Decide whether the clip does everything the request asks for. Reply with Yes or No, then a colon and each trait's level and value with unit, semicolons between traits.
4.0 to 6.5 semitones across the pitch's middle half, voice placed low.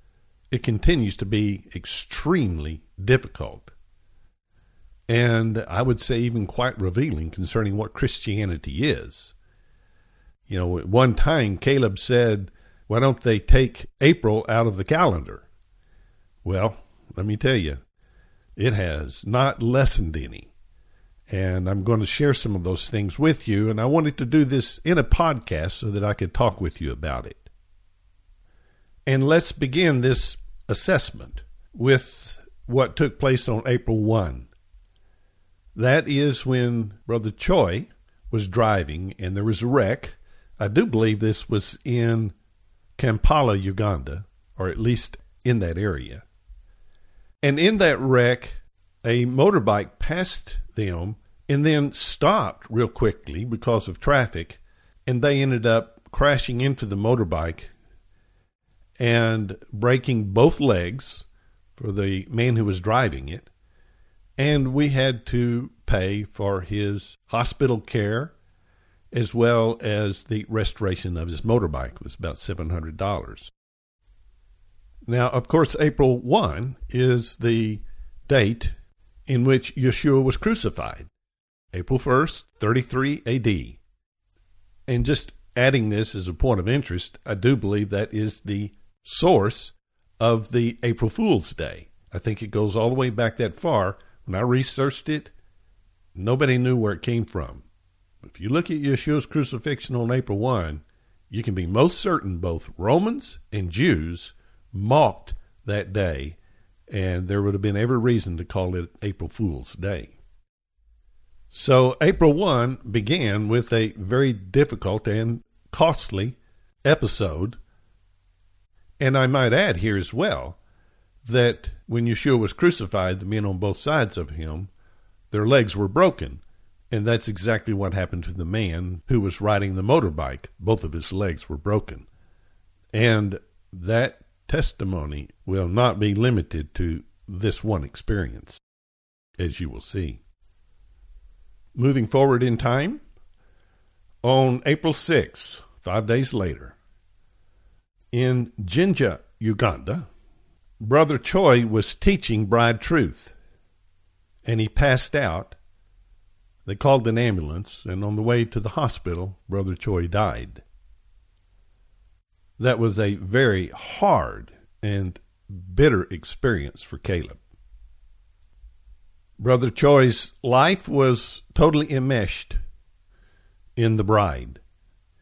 Yes: average, 5.1 semitones; low, 105 Hz